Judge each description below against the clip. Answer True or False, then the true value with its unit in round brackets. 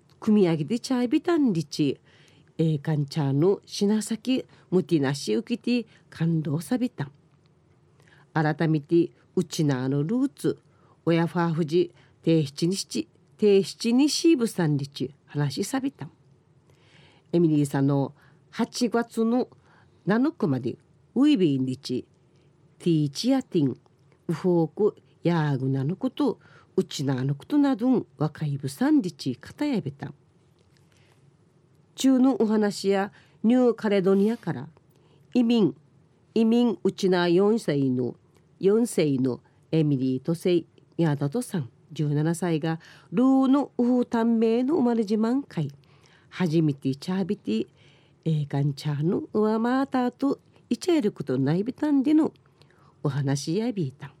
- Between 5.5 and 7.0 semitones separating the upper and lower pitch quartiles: False (7.8 semitones)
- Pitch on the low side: False (165 Hz)